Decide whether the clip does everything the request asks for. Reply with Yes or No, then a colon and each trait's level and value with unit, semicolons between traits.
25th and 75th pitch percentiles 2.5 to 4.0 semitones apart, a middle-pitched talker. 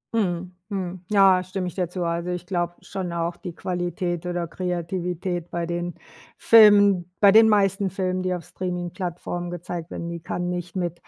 No: narrow, 1.3 semitones; medium, 180 Hz